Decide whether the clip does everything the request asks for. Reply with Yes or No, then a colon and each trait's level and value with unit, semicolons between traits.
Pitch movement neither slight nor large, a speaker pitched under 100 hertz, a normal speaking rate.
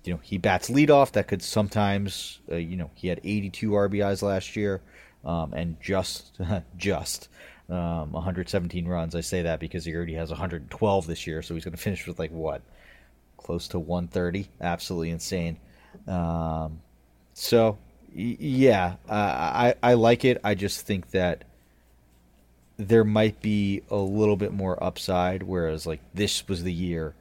Yes: average, 3.6 semitones; very low, 90 Hz; average, 165 wpm